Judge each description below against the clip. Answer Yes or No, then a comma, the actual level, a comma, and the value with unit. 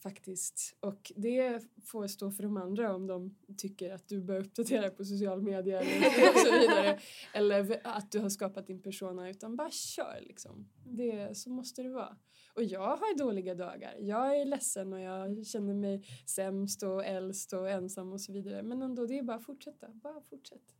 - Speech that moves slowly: No, average, 195 wpm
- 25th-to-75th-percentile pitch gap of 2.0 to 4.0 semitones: Yes, average, 3.3 semitones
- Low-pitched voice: No, high, 200 Hz